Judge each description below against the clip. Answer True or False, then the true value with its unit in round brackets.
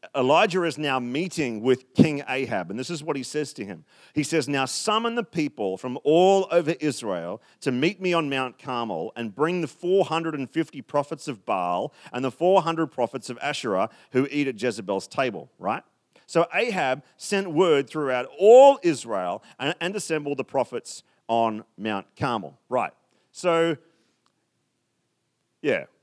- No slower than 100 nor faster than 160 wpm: True (155 wpm)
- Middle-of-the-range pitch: True (150 Hz)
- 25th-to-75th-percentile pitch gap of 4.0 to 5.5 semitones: True (4.8 semitones)